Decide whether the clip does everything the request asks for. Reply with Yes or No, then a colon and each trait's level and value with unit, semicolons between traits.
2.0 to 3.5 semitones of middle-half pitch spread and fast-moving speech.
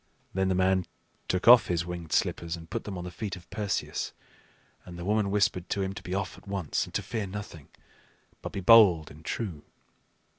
Yes: narrow, 2.6 semitones; fast, 210 wpm